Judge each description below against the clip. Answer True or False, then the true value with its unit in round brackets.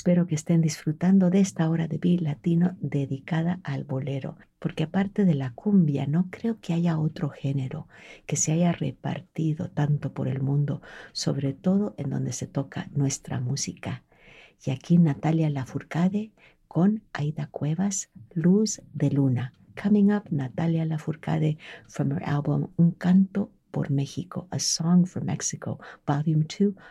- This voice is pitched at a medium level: True (160 Hz)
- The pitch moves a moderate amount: True (3.8 semitones)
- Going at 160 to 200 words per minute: False (150 wpm)